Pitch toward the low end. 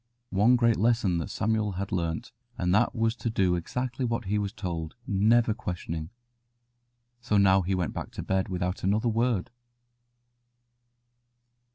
Yes: low, 105 Hz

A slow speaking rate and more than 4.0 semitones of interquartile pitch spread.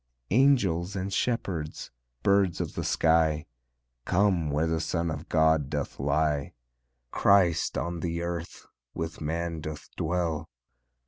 No: slow, 125 wpm; narrow, 2.4 semitones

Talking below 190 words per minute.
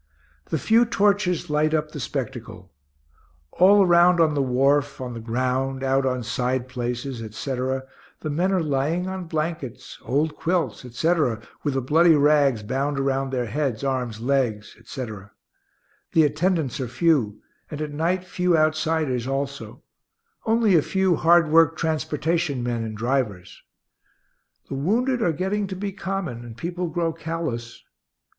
Yes: average, 150 wpm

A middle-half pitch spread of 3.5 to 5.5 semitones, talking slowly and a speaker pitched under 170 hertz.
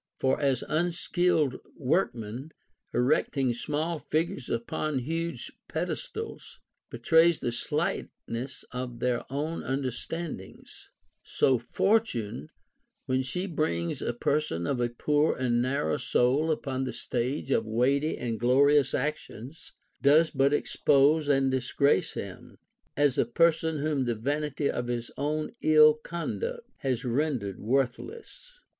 Yes: average, 4.1 semitones; slow, 125 wpm; medium, 140 Hz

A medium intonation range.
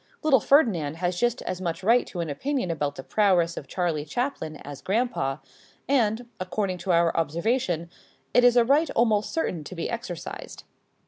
No: wide, 6.3 semitones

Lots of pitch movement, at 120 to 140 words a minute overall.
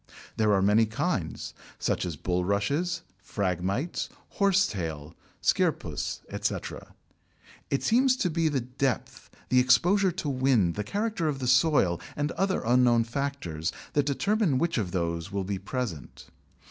Yes: wide, 8.5 semitones; slow, 135 wpm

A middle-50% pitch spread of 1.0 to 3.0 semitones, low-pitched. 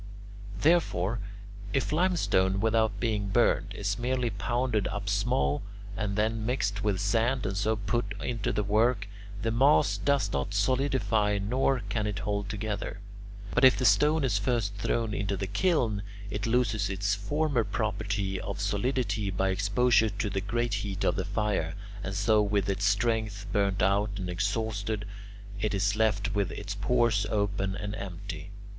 Yes: narrow, 2.6 semitones; low, 105 Hz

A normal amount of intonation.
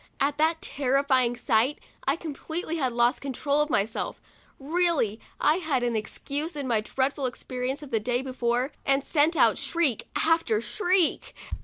Yes: average, 4.2 semitones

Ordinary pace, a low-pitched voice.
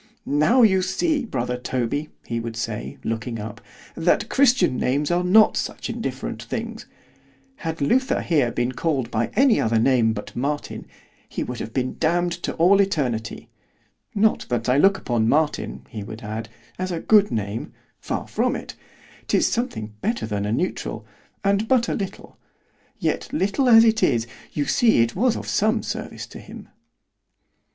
No: average, 155 wpm; medium, 150 Hz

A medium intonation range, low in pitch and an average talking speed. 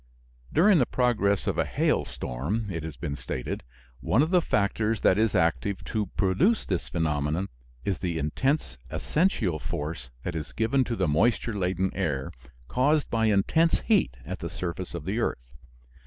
No: wide, 6.5 semitones; very low, 95 Hz; average, 165 wpm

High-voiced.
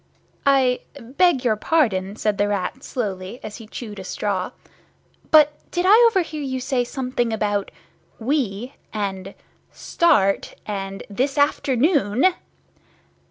Yes: high, 240 Hz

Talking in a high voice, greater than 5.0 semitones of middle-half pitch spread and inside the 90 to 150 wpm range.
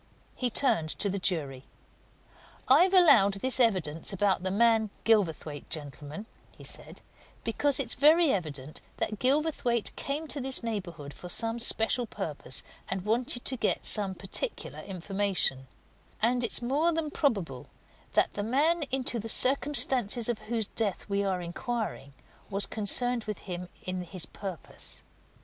Yes: high, 215 Hz; wide, 5.4 semitones; average, 140 wpm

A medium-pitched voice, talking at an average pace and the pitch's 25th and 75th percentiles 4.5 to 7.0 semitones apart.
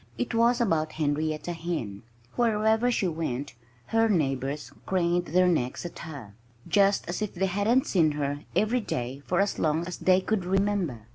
Yes: medium, 175 Hz; average, 165 wpm; wide, 5.4 semitones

